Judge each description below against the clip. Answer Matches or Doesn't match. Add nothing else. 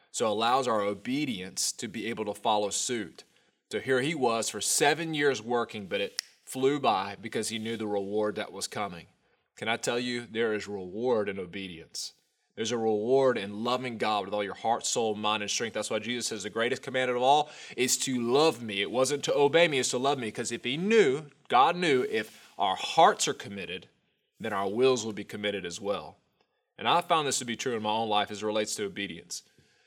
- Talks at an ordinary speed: Doesn't match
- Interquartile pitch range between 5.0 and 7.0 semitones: Doesn't match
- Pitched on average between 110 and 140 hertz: Matches